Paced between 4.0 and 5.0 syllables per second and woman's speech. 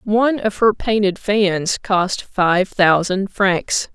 No: 3.2 syllables/s; female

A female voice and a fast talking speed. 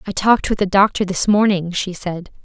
Yes: female; fast, 220 wpm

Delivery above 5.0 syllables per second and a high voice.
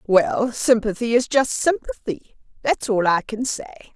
No: 4.3 syllables/s; high, 225 Hz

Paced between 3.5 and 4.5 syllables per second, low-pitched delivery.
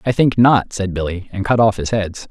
No: 5.1 syllables/s; low, 105 Hz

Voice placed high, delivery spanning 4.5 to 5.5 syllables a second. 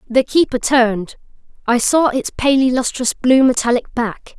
Yes: very high, 250 Hz; 4.8 syllables/s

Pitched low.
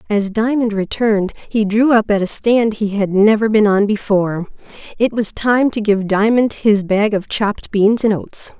No: high, 210 Hz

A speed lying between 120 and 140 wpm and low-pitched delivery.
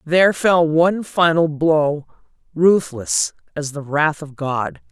No: slow, 135 wpm; medium, 160 Hz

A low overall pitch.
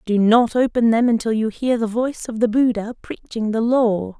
No: high, 225 Hz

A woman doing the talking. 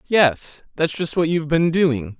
No: male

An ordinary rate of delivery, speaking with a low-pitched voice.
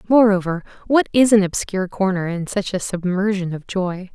No: average, 175 wpm; high, 195 Hz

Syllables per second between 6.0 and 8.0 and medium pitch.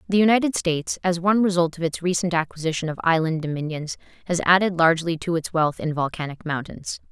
Yes: 6.2 syllables/s; medium, 170 Hz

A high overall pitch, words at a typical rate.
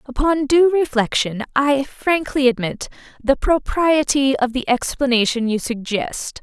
No: very high, 265 Hz; slow, 120 wpm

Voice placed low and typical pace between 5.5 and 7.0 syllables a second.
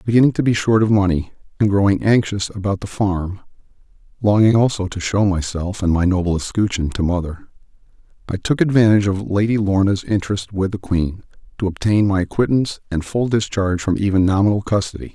Yes: low, 100 Hz; 5.9 syllables/s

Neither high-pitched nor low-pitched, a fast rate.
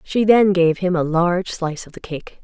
Yes: medium, 175 Hz; fast, 245 wpm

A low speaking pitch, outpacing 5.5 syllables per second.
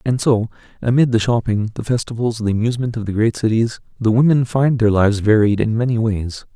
Yes: low, 115 Hz; 5.8 syllables/s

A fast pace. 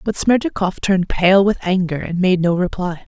No: average, 190 wpm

